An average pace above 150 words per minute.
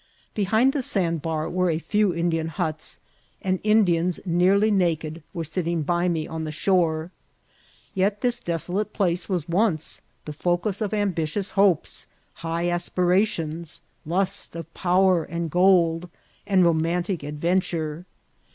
No: slow, 135 wpm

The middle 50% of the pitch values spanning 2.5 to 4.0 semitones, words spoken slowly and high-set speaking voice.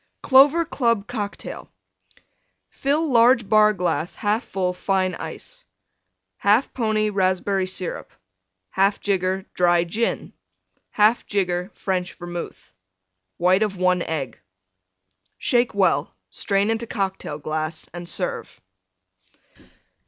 Yes: average, 3.4 semitones; slow, 105 wpm; high, 195 Hz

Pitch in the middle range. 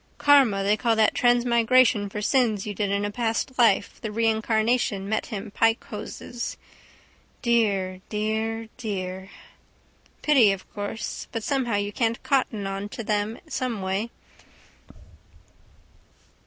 No: high, 220 Hz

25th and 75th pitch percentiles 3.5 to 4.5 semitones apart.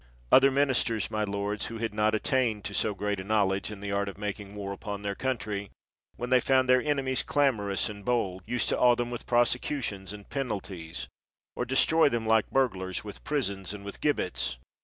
Yes: average, 3.9 semitones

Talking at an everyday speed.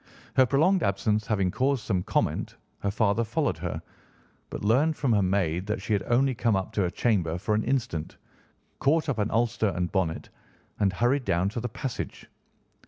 Yes: average, 185 wpm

